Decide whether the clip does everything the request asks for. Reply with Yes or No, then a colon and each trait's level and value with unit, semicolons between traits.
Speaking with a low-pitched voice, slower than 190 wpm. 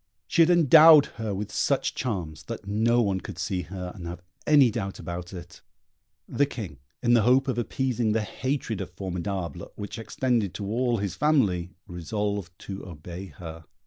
Yes: low, 100 Hz; average, 175 wpm